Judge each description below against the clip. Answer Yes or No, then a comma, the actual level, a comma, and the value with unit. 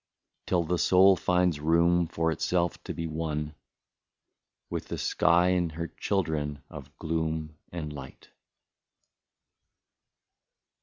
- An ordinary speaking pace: No, slow, 110 wpm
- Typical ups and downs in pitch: No, narrow, 2.0 semitones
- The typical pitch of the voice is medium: No, very low, 80 Hz